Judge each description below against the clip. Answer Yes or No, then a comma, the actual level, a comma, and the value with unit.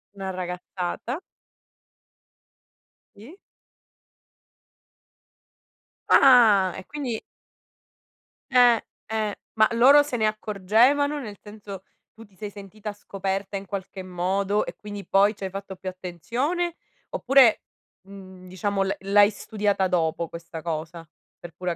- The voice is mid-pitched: No, high, 200 Hz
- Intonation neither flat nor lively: Yes, average, 3.0 semitones